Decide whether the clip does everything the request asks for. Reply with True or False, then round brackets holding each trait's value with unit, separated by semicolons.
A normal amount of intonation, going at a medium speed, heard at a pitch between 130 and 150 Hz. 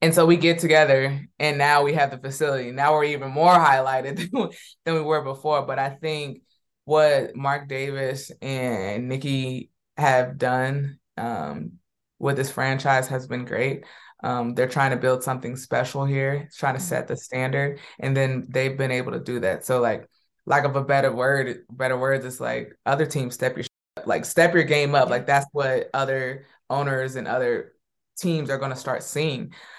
False (2.1 semitones; 185 wpm; 135 Hz)